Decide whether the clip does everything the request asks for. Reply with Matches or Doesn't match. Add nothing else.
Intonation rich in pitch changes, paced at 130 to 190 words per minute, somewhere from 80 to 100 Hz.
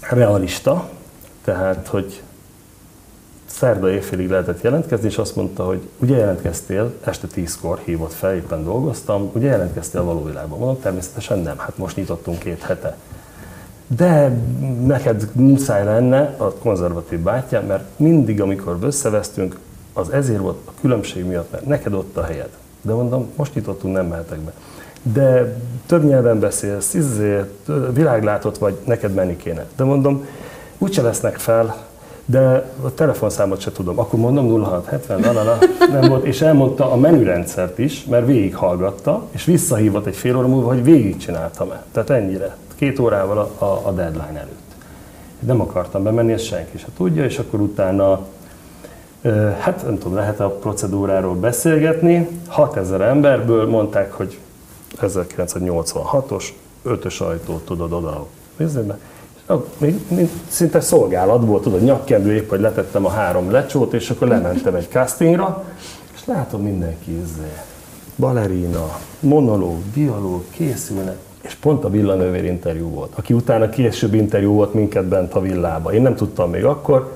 Doesn't match